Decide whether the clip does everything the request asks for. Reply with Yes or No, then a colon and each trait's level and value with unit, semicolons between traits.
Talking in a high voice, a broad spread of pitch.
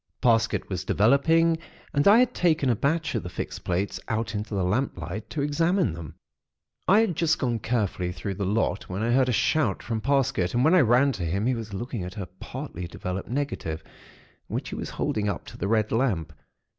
No: low, 115 Hz; wide, 6.4 semitones